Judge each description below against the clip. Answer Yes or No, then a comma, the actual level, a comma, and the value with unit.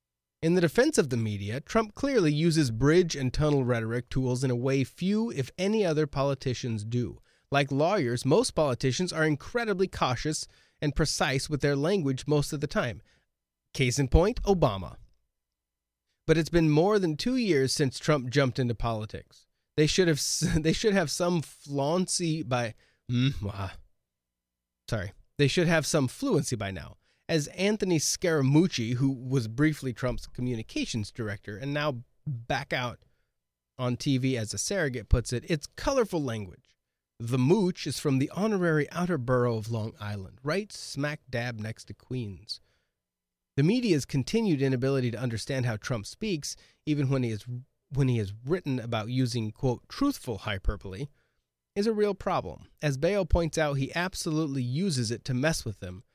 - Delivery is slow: No, average, 155 wpm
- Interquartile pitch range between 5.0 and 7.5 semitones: Yes, wide, 5.5 semitones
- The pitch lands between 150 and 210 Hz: No, low, 135 Hz